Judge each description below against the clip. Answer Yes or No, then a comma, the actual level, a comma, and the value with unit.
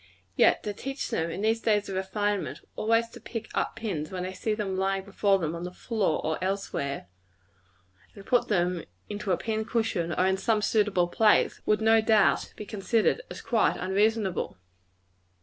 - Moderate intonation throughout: Yes, average, 3.0 semitones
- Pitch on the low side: No, high, 200 Hz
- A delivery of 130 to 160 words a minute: No, average, 180 wpm